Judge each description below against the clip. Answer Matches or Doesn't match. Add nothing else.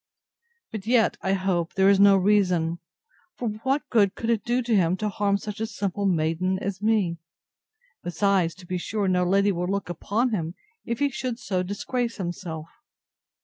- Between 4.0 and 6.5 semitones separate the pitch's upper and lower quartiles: Doesn't match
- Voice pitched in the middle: Doesn't match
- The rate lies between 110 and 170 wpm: Doesn't match